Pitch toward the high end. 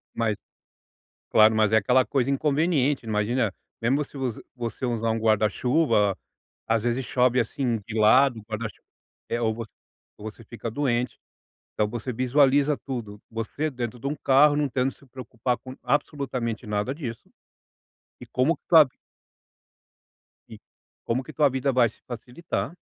No: low, 125 Hz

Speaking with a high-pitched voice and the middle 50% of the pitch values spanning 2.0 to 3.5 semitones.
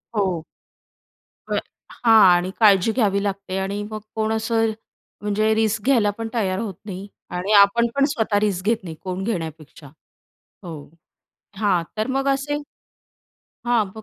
Yes: high, 210 Hz; average, 2.9 semitones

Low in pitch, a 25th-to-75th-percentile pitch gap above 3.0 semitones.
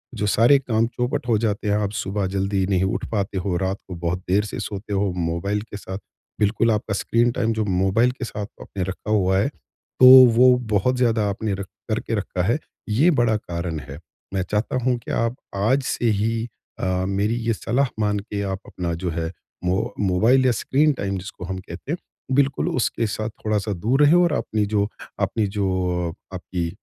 Yes: low, 105 Hz; average, 3.4 semitones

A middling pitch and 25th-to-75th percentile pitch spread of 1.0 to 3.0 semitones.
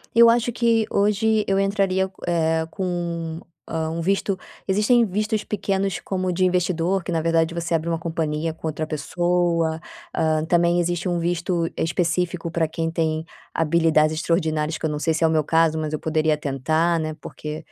Yes: medium, 170 Hz; average, 2.7 semitones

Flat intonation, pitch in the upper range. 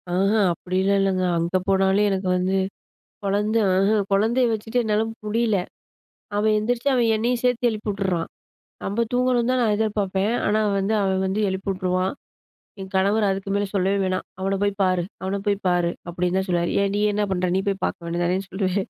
Yes: narrow, 2.3 semitones; high, 195 Hz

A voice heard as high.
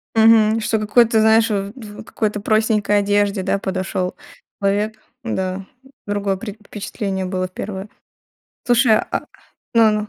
Yes: high, 210 Hz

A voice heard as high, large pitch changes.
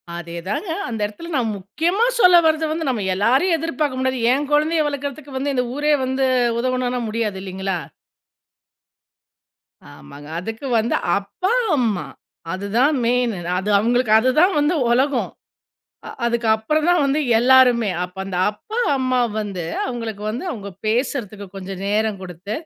Yes: high, 245 Hz; wide, 5.7 semitones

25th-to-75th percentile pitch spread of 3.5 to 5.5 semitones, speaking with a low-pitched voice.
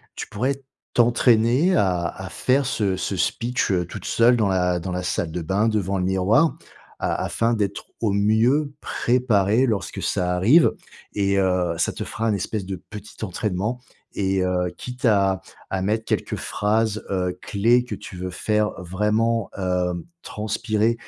Yes: average, 3.8 semitones; low, 105 Hz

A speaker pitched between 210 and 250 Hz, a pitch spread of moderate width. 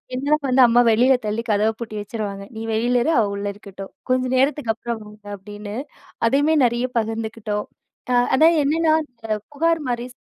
Yes: high, 230 Hz; average, 3.8 semitones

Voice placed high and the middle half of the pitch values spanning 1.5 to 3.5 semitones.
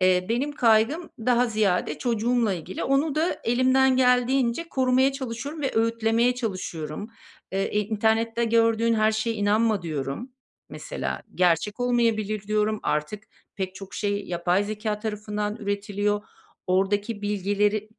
Yes: high, 215 Hz; average, 2.9 semitones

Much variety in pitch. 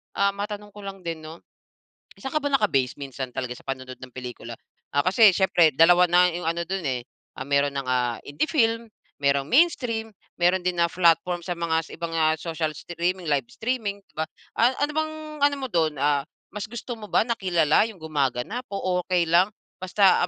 Yes: wide, 6.1 semitones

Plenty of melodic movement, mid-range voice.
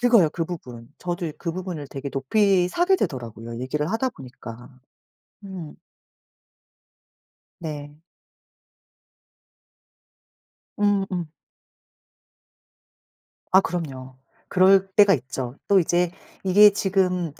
Yes: wide, 6.1 semitones; medium, 175 Hz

